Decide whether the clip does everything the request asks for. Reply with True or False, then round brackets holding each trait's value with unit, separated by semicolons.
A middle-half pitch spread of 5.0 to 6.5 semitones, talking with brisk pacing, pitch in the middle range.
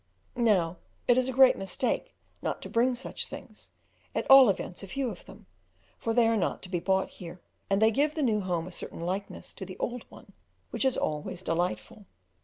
False (5.4 semitones; 210 wpm; 200 Hz)